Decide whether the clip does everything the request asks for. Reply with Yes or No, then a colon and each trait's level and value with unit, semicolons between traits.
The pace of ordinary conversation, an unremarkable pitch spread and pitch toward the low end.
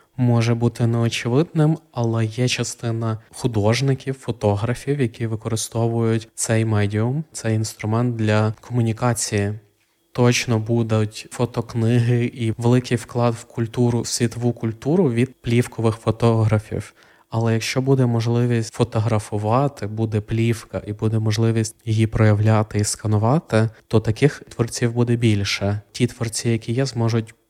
No: average, 120 wpm; narrow, 1.6 semitones; low, 115 Hz